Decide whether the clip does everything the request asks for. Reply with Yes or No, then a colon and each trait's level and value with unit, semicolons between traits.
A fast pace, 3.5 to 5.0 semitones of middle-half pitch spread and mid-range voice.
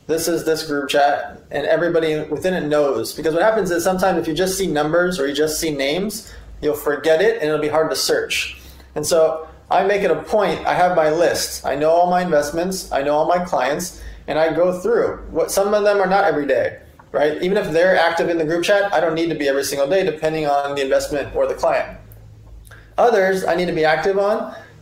Yes: fast, 235 wpm; average, 3.9 semitones; medium, 160 Hz